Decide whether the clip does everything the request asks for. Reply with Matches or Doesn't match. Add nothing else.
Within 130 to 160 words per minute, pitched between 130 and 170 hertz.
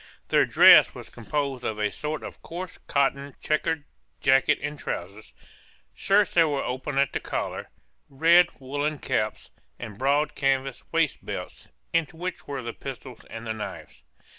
Matches